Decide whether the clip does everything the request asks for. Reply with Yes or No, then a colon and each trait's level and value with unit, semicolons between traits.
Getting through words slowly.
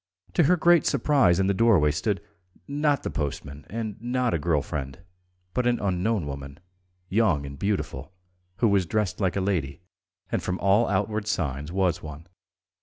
No: average, 170 wpm